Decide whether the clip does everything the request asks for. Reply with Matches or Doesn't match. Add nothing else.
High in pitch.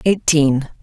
Doesn't match